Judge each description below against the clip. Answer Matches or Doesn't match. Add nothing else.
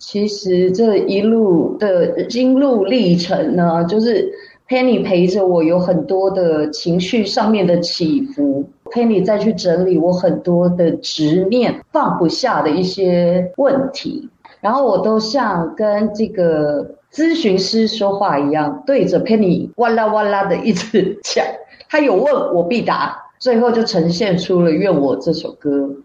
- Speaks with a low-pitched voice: Doesn't match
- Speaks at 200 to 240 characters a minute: Matches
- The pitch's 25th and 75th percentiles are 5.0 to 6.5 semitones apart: Matches